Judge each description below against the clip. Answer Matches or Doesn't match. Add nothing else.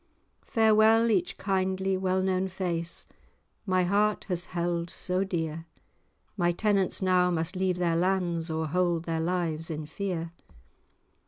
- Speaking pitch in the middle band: Matches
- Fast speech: Doesn't match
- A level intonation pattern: Matches